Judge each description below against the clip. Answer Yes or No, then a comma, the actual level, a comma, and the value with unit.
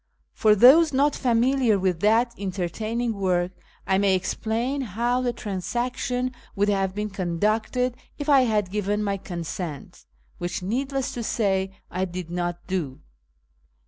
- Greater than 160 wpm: No, average, 140 wpm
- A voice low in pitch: No, high, 210 Hz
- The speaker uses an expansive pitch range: No, average, 4.5 semitones